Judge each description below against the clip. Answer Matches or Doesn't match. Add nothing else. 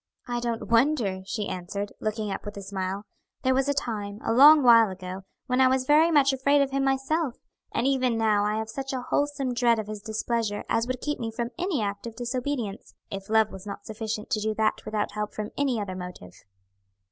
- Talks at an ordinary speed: Doesn't match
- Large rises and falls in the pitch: Doesn't match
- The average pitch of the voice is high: Matches